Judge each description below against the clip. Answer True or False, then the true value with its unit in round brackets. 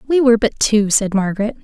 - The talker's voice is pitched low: False (220 Hz)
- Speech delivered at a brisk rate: True (220 wpm)